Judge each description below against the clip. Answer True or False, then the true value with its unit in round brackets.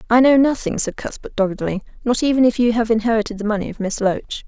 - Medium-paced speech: False (230 wpm)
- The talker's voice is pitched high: True (225 Hz)